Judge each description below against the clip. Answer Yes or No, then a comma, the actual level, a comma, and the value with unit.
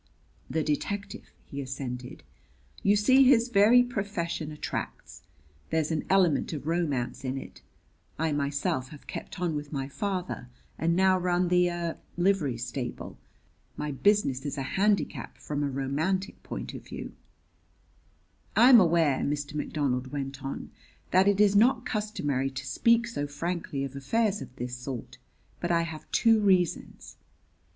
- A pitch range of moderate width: No, wide, 6.1 semitones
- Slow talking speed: No, average, 150 wpm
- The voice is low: No, medium, 160 Hz